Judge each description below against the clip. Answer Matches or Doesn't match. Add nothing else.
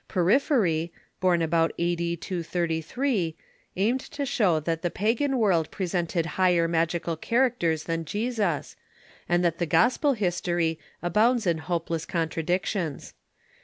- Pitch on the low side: Doesn't match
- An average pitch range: Matches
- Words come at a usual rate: Doesn't match